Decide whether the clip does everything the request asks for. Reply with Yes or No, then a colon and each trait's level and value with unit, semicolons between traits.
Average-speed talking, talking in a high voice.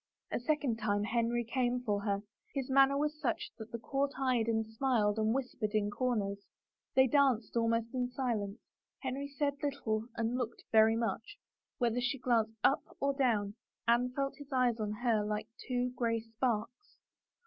Yes: average, 170 wpm; high, 235 Hz